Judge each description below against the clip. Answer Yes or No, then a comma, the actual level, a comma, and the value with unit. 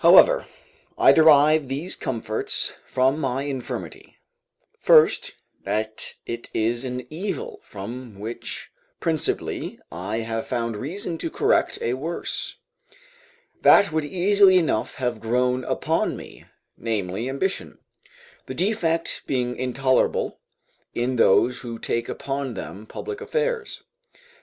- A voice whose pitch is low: Yes, low, 130 Hz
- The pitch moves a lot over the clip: Yes, wide, 6.0 semitones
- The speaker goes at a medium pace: No, slow, 115 wpm